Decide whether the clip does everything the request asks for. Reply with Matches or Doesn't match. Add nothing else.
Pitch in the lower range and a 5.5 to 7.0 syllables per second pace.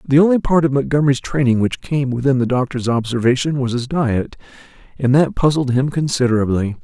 Matches